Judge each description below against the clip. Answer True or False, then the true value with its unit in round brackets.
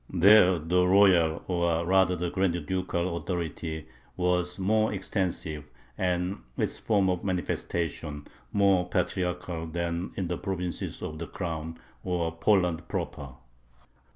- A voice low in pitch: True (90 Hz)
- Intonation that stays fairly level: True (1.9 semitones)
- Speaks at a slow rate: True (125 wpm)